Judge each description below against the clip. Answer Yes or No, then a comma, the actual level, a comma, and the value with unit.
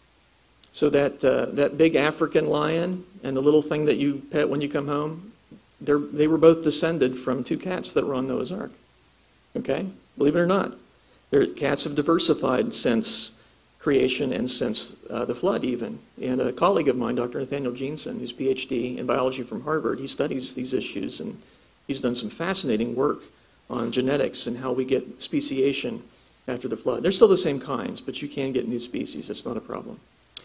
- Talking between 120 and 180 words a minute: No, average, 190 wpm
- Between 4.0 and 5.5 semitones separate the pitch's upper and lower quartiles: No, average, 3.2 semitones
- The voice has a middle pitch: Yes, medium, 145 Hz